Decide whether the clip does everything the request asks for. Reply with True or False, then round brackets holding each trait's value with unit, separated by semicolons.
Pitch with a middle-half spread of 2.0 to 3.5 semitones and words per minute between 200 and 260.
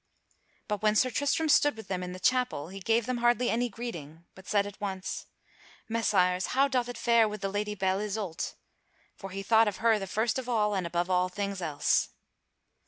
False (3.9 semitones; 205 wpm)